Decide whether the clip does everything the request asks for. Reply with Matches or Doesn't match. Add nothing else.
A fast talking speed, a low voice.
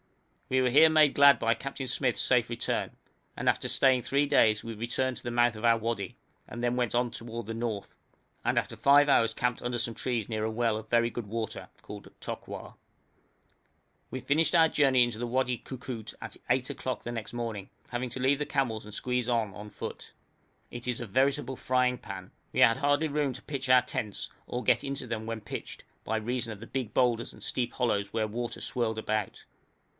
Matches